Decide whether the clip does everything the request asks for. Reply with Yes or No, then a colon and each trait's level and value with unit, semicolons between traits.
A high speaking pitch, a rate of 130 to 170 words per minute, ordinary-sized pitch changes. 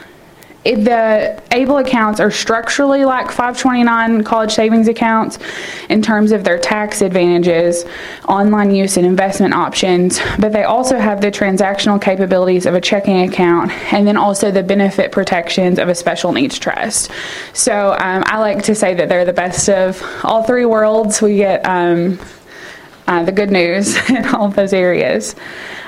Yes: high, 205 Hz; average, 160 wpm; average, 3.3 semitones